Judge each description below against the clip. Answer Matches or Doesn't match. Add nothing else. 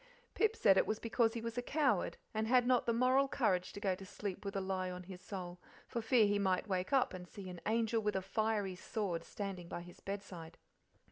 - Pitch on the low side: Doesn't match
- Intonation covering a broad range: Doesn't match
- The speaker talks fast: Matches